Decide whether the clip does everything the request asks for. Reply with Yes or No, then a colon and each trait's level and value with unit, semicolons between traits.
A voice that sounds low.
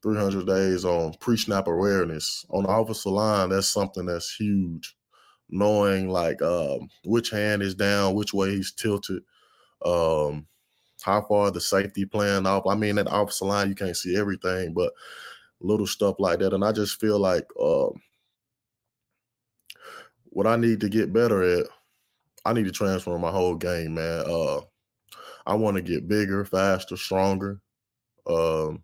Yes: low, 100 Hz